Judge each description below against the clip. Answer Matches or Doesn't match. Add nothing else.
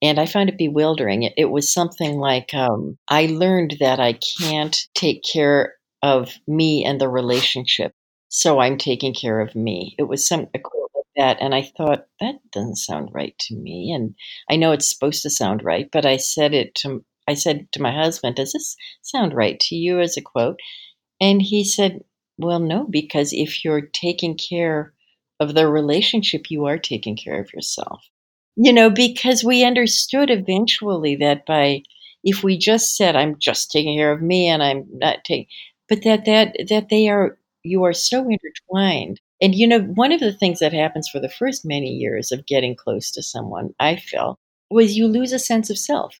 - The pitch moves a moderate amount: Doesn't match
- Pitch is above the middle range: Doesn't match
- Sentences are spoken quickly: Doesn't match